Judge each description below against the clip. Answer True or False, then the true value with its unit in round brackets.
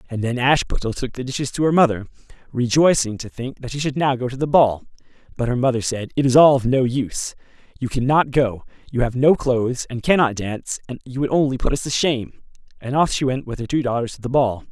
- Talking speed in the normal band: False (240 wpm)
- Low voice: True (130 Hz)